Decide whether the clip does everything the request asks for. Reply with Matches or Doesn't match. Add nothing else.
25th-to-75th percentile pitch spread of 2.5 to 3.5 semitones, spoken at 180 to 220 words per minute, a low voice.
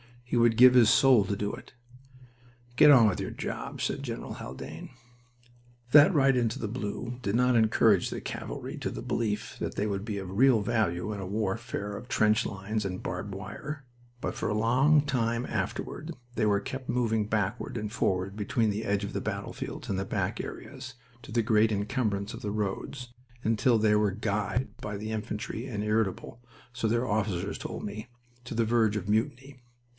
Matches